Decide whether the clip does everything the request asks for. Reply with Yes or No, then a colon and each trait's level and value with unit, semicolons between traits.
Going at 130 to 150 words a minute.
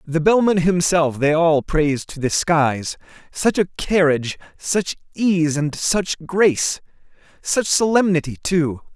Yes: slow, 135 wpm